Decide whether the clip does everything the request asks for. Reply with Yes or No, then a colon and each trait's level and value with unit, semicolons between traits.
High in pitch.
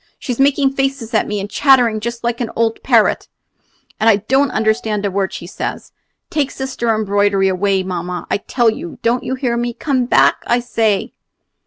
Yes: high, 225 Hz